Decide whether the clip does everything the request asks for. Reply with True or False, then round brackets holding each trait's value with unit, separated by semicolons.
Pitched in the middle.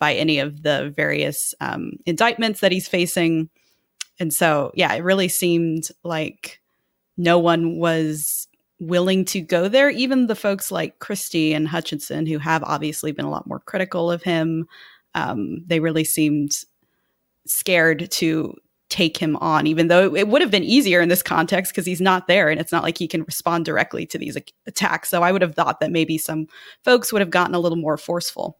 True (170 Hz)